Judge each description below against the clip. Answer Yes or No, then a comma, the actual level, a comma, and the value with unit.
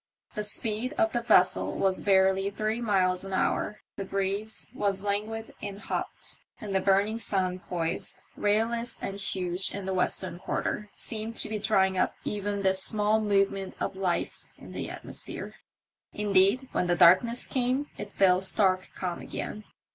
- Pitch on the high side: Yes, high, 200 Hz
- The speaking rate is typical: Yes, average, 160 wpm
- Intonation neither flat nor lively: No, narrow, 2.1 semitones